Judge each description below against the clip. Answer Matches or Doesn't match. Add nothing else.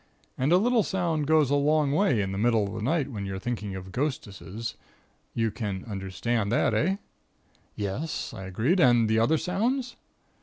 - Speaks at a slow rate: Doesn't match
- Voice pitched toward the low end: Matches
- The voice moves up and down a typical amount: Doesn't match